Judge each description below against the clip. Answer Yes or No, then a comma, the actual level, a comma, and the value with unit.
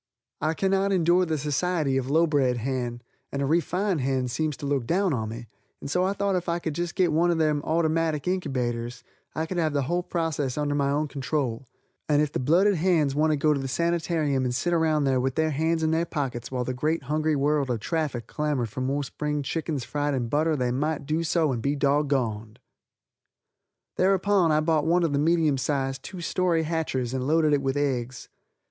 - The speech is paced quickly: Yes, fast, 215 wpm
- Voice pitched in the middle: Yes, medium, 150 Hz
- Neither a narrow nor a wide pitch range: Yes, average, 3.5 semitones